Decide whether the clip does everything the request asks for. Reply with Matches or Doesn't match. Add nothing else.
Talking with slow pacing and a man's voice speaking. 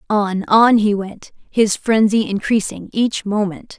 Doesn't match